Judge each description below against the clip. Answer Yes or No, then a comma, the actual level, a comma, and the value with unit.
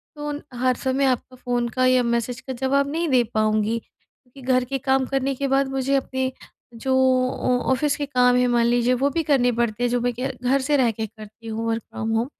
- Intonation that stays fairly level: Yes, narrow, 2.2 semitones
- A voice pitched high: Yes, very high, 255 Hz